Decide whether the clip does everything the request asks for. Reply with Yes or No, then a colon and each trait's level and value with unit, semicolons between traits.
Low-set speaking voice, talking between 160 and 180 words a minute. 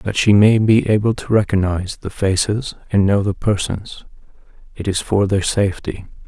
Yes: low, 100 Hz; average, 170 wpm